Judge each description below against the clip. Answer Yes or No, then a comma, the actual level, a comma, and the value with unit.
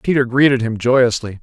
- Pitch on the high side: No, low, 125 Hz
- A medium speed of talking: Yes, average, 170 wpm